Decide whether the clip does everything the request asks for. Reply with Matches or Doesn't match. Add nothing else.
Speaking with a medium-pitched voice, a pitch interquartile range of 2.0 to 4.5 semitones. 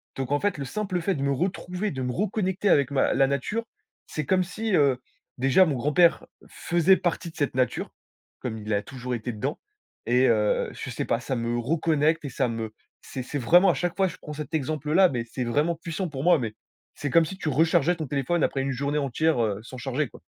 Doesn't match